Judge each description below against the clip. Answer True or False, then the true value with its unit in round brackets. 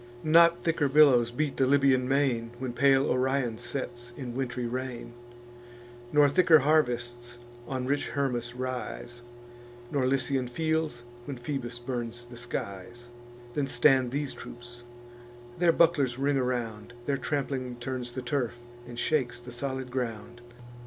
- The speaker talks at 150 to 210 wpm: False (135 wpm)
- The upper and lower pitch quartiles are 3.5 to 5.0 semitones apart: False (2.5 semitones)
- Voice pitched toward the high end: False (130 Hz)